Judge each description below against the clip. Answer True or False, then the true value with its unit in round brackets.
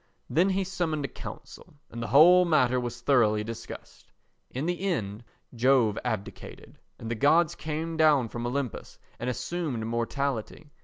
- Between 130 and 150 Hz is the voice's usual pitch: True (135 Hz)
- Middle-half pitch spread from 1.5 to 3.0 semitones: False (5.3 semitones)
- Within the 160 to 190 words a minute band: False (150 wpm)